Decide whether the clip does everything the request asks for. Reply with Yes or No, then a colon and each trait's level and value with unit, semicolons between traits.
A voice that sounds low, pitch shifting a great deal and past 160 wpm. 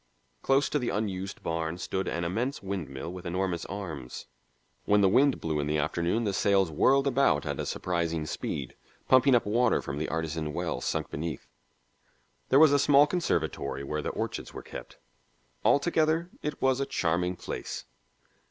Yes: very low, 95 Hz; wide, 8.3 semitones; average, 170 wpm